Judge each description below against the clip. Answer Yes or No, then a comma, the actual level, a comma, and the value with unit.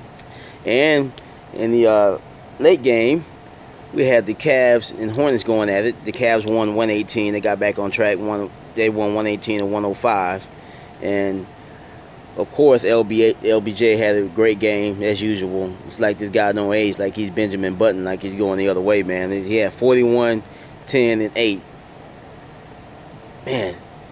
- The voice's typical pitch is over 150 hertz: No, low, 105 Hz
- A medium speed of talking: Yes, average, 160 wpm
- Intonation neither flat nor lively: No, narrow, 2.0 semitones